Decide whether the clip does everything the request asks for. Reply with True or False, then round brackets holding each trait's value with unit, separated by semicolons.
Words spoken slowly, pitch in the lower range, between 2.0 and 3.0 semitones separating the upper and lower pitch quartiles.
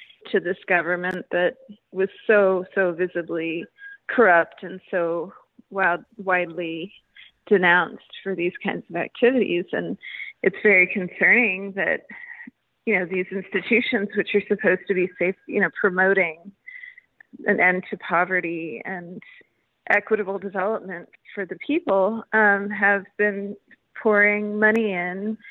False (125 wpm; 195 Hz; 2.7 semitones)